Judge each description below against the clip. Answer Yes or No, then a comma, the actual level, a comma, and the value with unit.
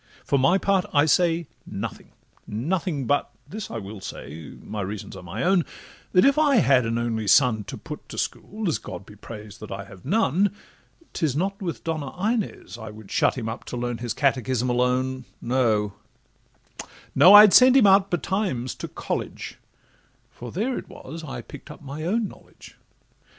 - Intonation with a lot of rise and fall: Yes, wide, 8.7 semitones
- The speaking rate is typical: Yes, average, 165 wpm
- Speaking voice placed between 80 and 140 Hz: Yes, low, 135 Hz